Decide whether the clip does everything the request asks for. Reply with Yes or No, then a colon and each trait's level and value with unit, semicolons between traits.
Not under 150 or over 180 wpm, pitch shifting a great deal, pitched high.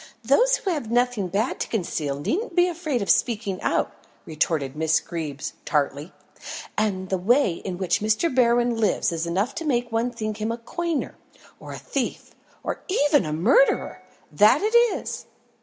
Yes: average, 170 wpm; wide, 7.5 semitones; high, 225 Hz